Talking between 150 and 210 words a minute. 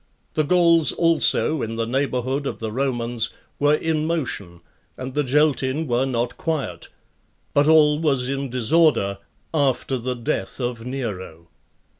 No: average, 140 wpm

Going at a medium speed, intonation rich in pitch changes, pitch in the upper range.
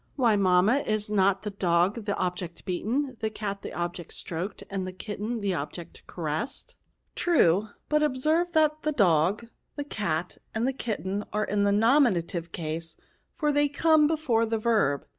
Yes: average, 175 wpm; wide, 6.4 semitones; high, 210 Hz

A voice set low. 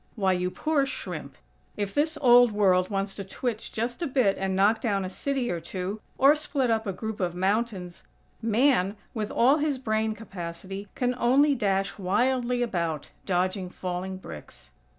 No: high, 210 Hz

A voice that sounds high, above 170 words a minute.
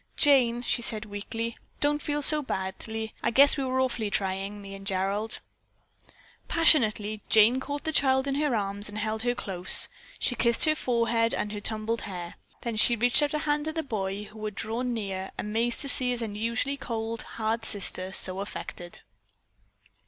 Yes: high, 225 Hz; average, 180 wpm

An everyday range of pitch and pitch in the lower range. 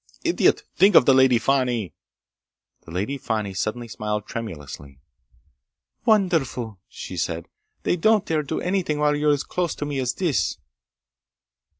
No: wide, 6.7 semitones; low, 130 Hz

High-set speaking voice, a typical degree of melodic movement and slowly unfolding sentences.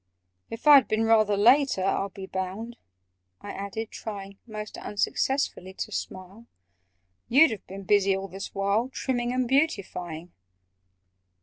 Yes: high, 210 Hz; average, 3.6 semitones; slow, 130 wpm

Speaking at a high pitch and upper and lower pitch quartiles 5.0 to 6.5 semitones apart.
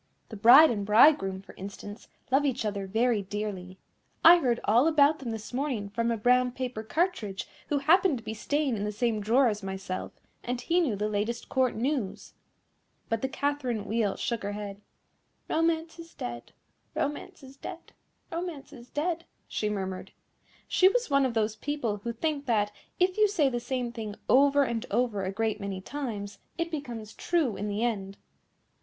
Yes: high, 235 Hz; wide, 5.6 semitones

